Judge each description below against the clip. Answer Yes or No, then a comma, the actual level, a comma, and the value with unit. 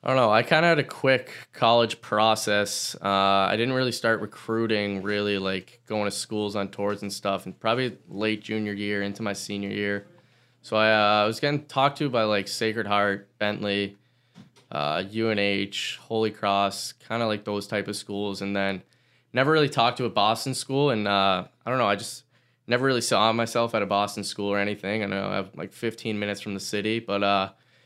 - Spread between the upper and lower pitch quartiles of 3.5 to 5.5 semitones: No, narrow, 2.5 semitones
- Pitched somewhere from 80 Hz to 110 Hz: Yes, low, 105 Hz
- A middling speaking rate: No, fast, 210 wpm